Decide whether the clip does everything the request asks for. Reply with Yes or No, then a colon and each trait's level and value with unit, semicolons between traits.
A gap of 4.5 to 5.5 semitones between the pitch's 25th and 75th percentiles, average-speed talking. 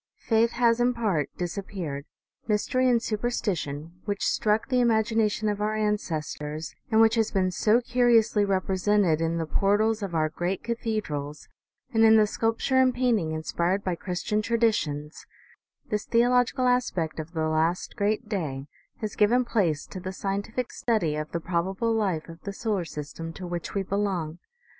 Yes: average, 5.1 semitones; average, 165 wpm